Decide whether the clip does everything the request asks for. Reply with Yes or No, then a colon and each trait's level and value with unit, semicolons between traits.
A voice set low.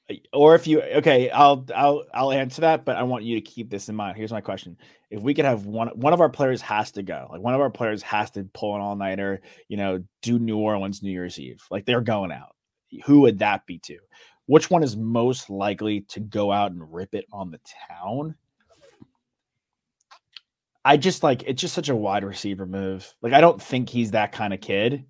Yes: low, 110 Hz